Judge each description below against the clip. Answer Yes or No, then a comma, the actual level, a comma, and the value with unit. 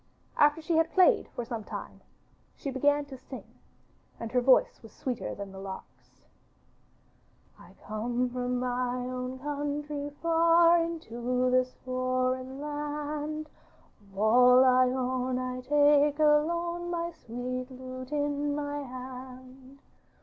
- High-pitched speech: Yes, very high, 260 Hz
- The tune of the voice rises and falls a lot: No, average, 2.8 semitones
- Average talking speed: No, slow, 130 wpm